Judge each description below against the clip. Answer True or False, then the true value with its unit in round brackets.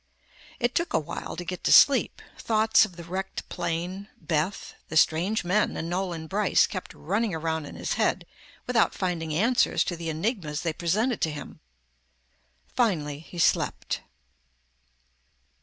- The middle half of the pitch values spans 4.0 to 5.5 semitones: True (4.6 semitones)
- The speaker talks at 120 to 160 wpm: True (145 wpm)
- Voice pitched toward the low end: False (175 Hz)